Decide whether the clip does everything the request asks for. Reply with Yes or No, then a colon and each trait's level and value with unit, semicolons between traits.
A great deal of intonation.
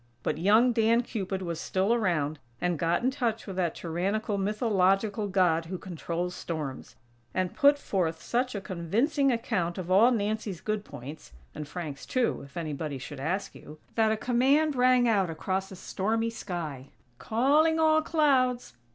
Yes: wide, 5.8 semitones